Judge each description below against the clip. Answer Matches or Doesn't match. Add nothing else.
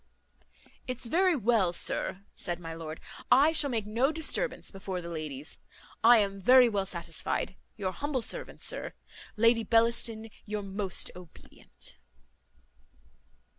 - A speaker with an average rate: Doesn't match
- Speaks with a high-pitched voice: Matches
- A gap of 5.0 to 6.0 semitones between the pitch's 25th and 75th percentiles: Matches